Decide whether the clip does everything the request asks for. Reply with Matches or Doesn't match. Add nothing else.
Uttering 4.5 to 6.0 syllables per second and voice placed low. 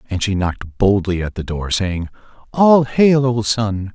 Doesn't match